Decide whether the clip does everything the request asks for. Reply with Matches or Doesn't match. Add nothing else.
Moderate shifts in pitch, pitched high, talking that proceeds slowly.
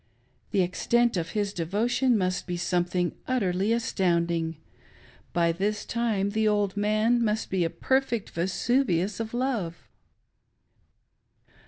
Matches